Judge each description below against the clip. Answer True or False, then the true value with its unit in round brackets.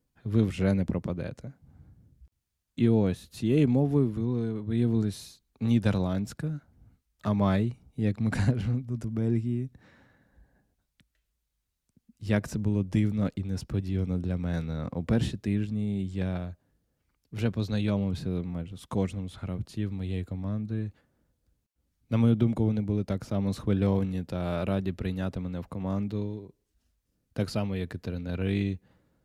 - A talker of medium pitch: False (100 Hz)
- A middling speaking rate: False (115 wpm)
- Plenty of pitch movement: False (3.0 semitones)